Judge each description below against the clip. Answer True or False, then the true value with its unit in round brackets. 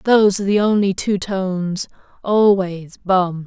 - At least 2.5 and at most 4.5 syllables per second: True (4.4 syllables/s)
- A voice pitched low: False (190 Hz)